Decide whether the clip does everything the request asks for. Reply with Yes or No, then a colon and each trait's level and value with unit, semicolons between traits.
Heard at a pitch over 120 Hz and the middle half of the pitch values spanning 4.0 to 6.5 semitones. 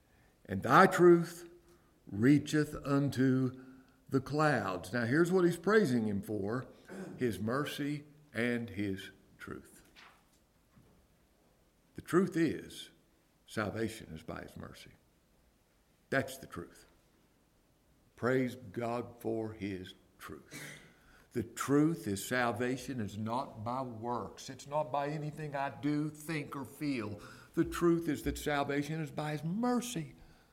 Yes: low, 135 Hz; average, 5.1 semitones